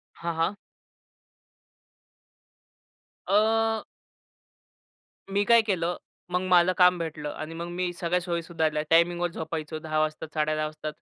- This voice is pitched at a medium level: Yes, medium, 170 Hz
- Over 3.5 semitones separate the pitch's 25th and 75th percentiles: No, narrow, 2.6 semitones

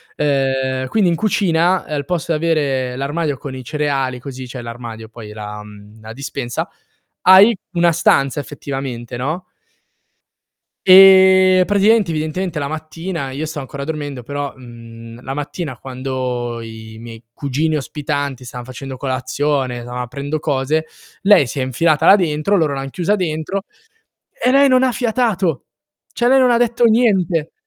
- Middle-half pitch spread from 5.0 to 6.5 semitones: Yes, average, 5.3 semitones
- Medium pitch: Yes, medium, 145 Hz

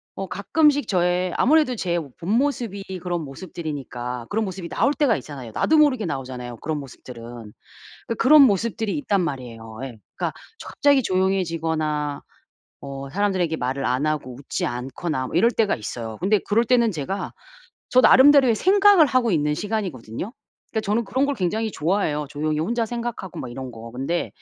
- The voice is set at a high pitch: No, medium, 175 Hz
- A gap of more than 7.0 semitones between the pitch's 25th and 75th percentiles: Yes, wide, 8.8 semitones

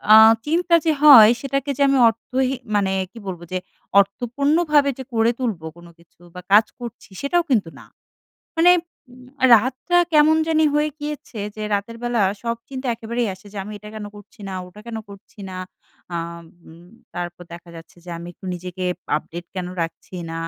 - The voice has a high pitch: Yes, high, 225 Hz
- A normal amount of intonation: No, wide, 7.1 semitones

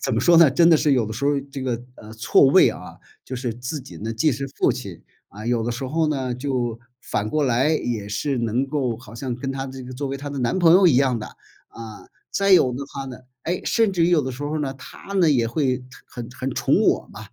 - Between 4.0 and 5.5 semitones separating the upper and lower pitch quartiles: No, average, 3.5 semitones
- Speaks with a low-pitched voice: Yes, low, 130 Hz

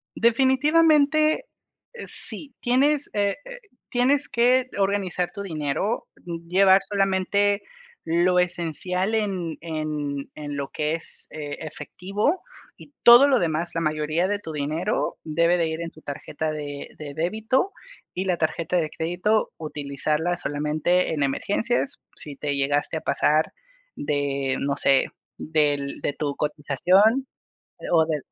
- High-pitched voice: No, medium, 170 Hz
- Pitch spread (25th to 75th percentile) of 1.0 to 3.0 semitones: No, wide, 5.5 semitones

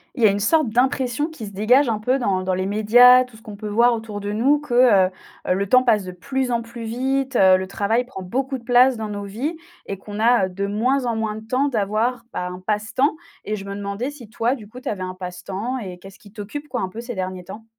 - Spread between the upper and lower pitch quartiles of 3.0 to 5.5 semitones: Yes, average, 3.9 semitones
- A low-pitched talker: No, high, 220 Hz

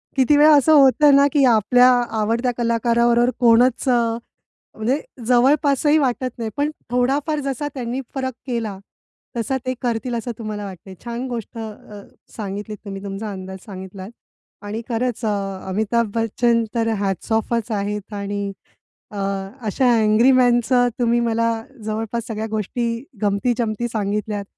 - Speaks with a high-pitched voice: Yes, high, 230 Hz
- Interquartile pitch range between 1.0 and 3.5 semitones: Yes, average, 2.9 semitones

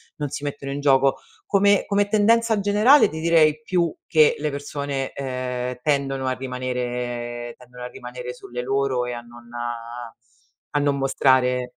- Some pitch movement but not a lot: Yes, average, 3.6 semitones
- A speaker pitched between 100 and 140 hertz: Yes, low, 135 Hz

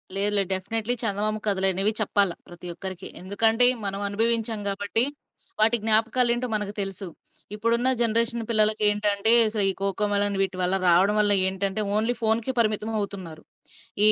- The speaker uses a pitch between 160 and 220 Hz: Yes, high, 210 Hz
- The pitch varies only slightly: Yes, narrow, 2.3 semitones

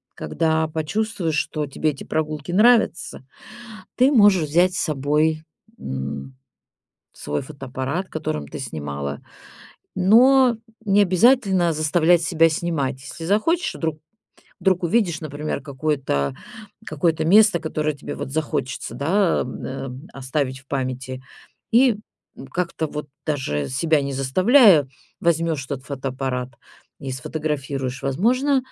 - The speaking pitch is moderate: Yes, medium, 155 Hz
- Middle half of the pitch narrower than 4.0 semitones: No, average, 5.2 semitones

